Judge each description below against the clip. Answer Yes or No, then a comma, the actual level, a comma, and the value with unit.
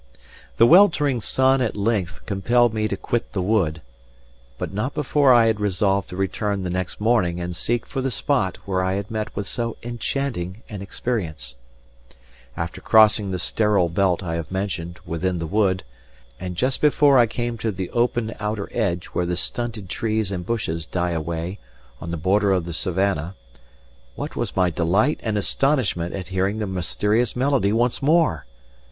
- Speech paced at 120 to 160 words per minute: No, average, 175 wpm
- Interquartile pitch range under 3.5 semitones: No, average, 4.6 semitones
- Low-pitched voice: Yes, low, 100 Hz